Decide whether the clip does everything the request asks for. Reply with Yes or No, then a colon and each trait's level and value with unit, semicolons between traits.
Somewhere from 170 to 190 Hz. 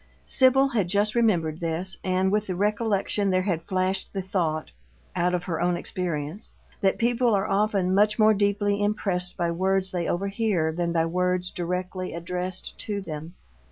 Yes: medium, 185 Hz